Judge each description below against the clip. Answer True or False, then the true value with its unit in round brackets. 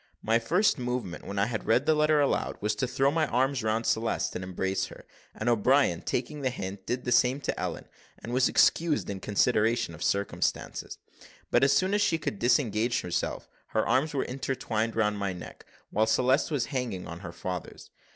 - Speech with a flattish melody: False (4.6 semitones)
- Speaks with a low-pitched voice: True (120 Hz)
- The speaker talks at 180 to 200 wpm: True (195 wpm)